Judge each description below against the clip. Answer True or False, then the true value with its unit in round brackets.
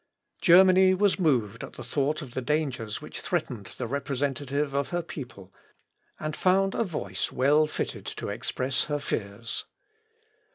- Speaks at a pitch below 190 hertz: True (140 Hz)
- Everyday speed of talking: True (155 wpm)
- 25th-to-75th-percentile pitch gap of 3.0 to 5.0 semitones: True (4.5 semitones)